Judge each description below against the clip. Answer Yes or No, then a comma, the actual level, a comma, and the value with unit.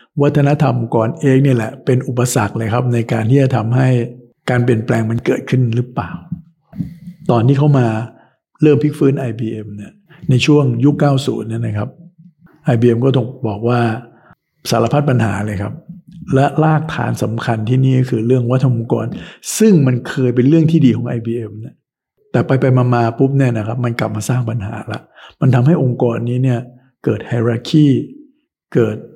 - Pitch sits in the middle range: No, low, 125 Hz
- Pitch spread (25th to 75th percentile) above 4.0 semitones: No, average, 3.7 semitones